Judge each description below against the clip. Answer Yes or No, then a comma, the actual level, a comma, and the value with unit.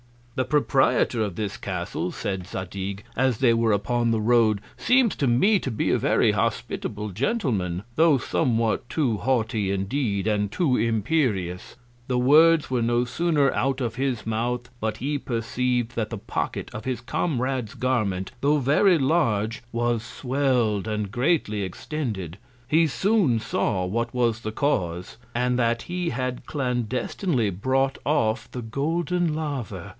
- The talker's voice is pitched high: No, low, 120 Hz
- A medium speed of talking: Yes, average, 150 wpm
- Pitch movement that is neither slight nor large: Yes, average, 4.3 semitones